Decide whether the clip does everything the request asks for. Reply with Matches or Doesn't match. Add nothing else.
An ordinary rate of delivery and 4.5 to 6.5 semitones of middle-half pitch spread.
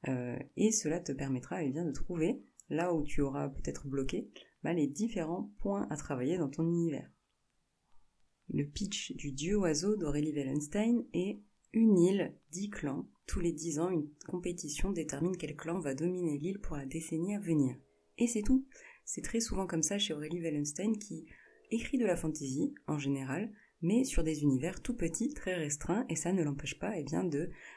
Matches